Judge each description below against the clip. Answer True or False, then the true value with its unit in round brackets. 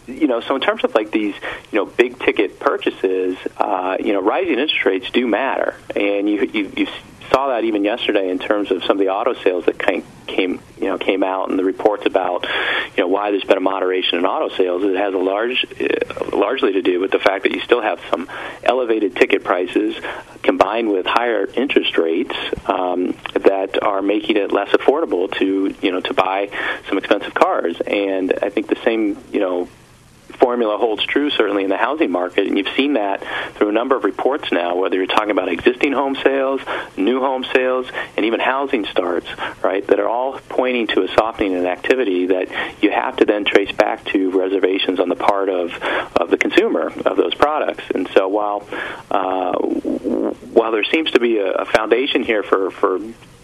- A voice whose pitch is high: False (130 Hz)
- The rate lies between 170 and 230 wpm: True (200 wpm)